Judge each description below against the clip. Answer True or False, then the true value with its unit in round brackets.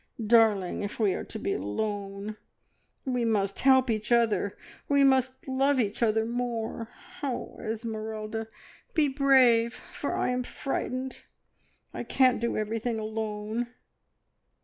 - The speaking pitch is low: False (230 Hz)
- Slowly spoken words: True (125 wpm)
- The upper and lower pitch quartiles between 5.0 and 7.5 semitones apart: False (2.9 semitones)